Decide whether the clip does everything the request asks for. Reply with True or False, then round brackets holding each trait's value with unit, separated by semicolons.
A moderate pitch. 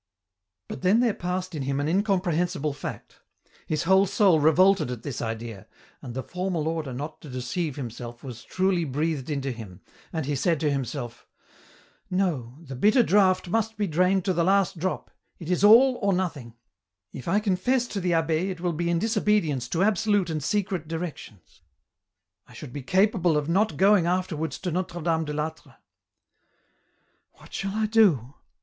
True (170 Hz)